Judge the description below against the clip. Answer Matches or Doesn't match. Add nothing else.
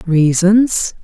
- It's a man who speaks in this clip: Doesn't match